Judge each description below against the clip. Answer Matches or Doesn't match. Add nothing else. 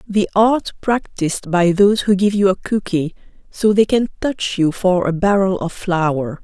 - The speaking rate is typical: Matches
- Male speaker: Doesn't match